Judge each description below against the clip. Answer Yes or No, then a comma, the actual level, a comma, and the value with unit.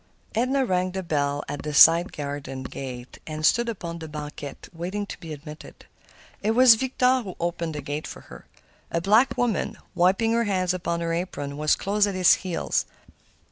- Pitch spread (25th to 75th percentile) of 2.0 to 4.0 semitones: No, wide, 5.4 semitones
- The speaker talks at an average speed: Yes, average, 180 wpm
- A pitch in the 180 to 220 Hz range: No, medium, 170 Hz